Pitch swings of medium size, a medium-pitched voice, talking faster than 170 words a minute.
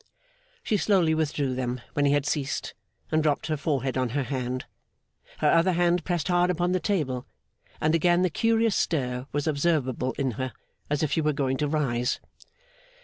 Yes: average, 4.7 semitones; medium, 150 Hz; average, 180 wpm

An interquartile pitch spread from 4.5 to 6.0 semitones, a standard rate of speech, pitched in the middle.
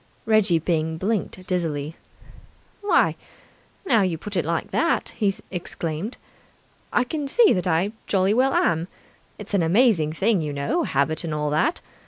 Yes: average, 5.2 semitones; average, 155 wpm; medium, 180 Hz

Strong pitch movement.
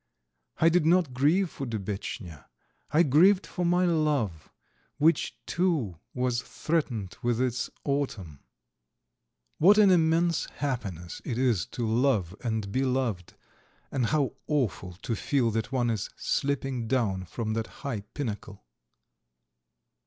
Yes: wide, 5.8 semitones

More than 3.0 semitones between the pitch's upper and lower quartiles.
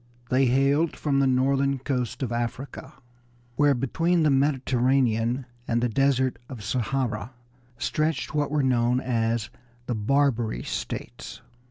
No: narrow, 2.5 semitones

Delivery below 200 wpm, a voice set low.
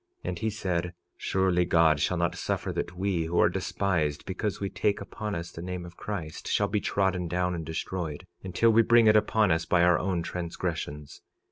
No: fast, 205 wpm; very low, 90 Hz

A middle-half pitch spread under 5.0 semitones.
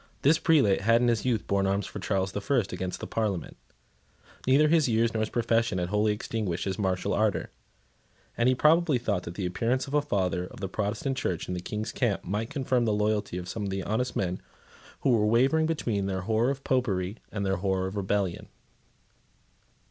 Yes: average, 4.1 semitones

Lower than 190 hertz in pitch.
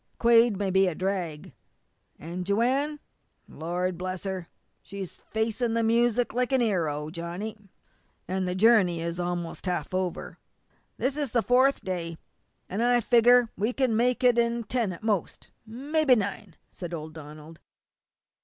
No: high, 200 Hz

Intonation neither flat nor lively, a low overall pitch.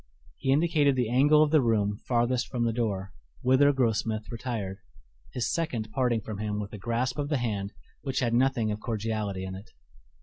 Yes: average, 3.6 semitones; low, 115 Hz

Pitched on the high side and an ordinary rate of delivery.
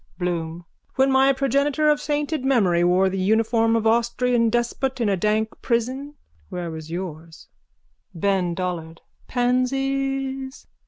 No: high, 230 Hz; slow, 130 wpm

